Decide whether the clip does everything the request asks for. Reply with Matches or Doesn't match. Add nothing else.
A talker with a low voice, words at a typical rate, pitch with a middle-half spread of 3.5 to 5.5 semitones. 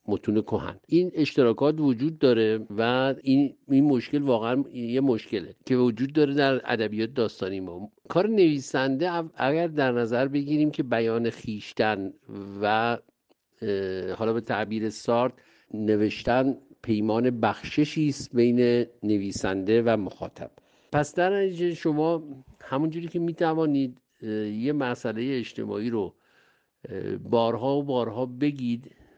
Matches